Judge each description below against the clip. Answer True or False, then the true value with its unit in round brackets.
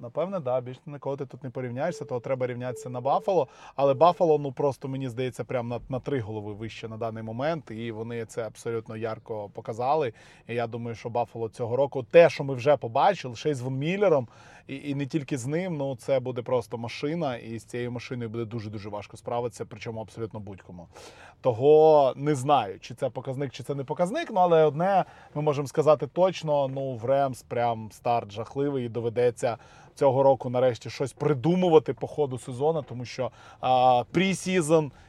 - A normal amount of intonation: True (3.8 semitones)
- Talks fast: True (190 wpm)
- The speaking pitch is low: True (130 Hz)